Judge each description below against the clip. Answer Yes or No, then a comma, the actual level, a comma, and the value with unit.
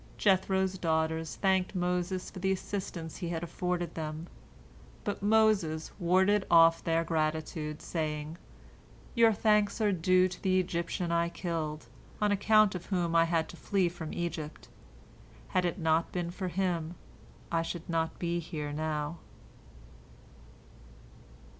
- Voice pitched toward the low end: No, medium, 175 Hz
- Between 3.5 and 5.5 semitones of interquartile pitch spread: No, narrow, 2.6 semitones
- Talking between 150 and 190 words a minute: No, slow, 135 wpm